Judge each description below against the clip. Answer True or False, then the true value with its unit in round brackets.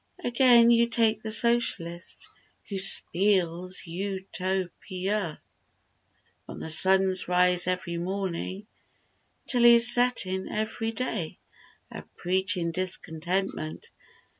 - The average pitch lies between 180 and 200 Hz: True (190 Hz)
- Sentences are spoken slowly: True (105 wpm)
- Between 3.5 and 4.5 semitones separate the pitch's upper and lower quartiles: True (3.8 semitones)